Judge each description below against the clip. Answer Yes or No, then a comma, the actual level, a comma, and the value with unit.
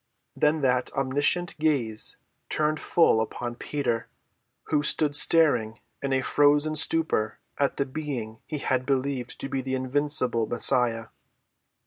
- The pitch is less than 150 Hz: Yes, low, 135 Hz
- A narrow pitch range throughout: No, average, 3.4 semitones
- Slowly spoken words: Yes, slow, 130 wpm